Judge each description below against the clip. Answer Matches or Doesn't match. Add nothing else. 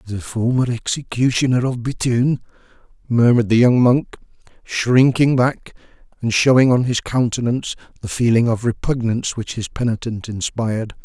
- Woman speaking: Doesn't match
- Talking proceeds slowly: Matches